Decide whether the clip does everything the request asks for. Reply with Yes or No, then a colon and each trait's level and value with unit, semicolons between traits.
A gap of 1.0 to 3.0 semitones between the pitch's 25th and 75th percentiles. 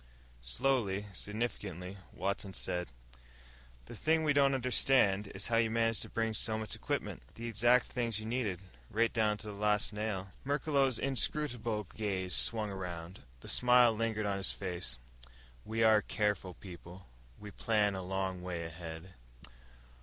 No: average, 3.5 semitones